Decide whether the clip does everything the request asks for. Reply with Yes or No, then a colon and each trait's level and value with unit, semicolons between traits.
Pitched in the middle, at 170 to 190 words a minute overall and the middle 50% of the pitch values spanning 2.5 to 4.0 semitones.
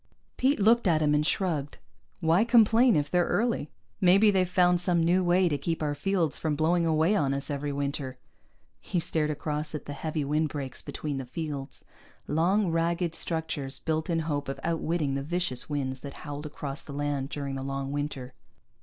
Yes: medium, 155 Hz; average, 185 wpm; average, 3.5 semitones